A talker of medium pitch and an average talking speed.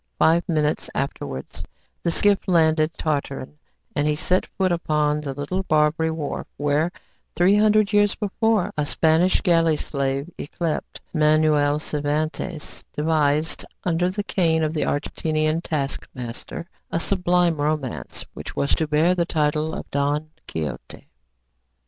No: medium, 155 Hz; slow, 130 wpm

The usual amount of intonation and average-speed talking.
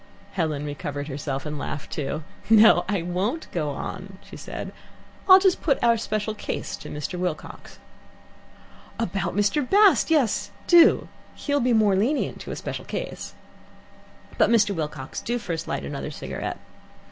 No: wide, 7.4 semitones; average, 150 wpm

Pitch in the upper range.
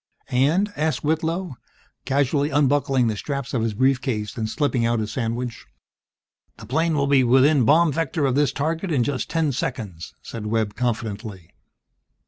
No: low, 135 Hz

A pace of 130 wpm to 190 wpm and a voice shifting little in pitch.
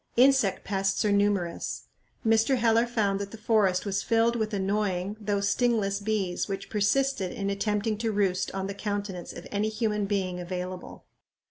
Yes: average, 165 wpm; narrow, 2.1 semitones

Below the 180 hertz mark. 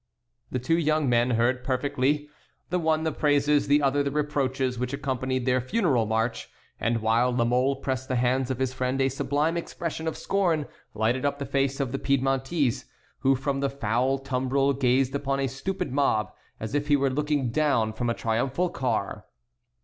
Yes: low, 135 Hz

